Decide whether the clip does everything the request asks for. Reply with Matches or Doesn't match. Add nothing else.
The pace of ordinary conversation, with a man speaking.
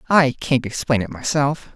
Matches